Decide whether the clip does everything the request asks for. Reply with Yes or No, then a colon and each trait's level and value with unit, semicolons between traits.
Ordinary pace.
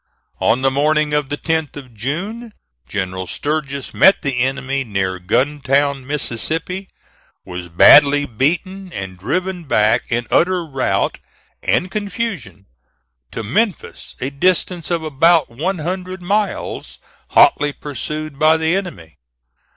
No: slow, 125 wpm